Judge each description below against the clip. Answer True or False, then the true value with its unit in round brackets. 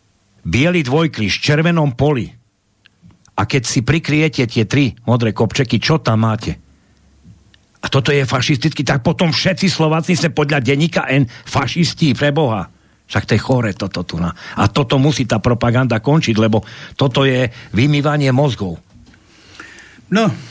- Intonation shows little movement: False (5.1 semitones)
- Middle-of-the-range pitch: False (130 Hz)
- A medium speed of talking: True (140 wpm)